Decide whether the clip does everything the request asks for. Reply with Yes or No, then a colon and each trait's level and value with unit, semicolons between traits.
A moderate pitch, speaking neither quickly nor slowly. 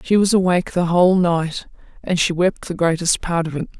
No: medium, 175 Hz; fast, 220 wpm